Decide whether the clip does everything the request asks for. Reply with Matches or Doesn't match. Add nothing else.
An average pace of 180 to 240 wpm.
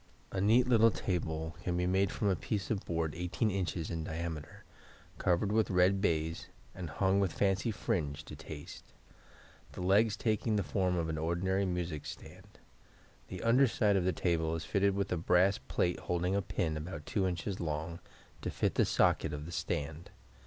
Matches